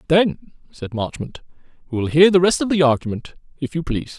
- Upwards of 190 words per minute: Yes, average, 200 wpm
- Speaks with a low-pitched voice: No, medium, 155 Hz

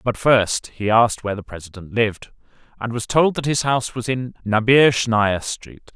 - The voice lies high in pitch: No, low, 115 Hz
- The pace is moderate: Yes, average, 180 wpm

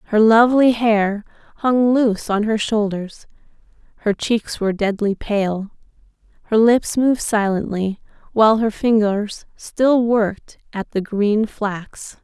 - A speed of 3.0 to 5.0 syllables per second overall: Yes, 4.0 syllables/s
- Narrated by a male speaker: No, female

